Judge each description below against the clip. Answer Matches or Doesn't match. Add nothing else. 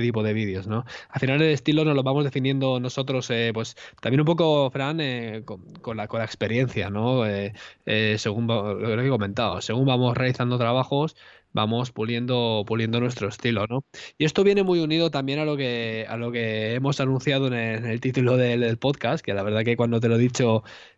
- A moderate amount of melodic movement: Matches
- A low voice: Matches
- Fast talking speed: Matches